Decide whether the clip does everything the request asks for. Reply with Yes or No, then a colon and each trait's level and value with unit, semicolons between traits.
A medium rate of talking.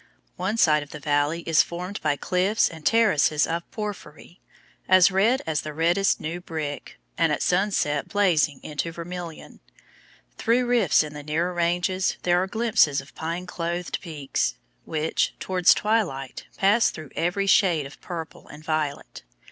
Yes: average, 155 wpm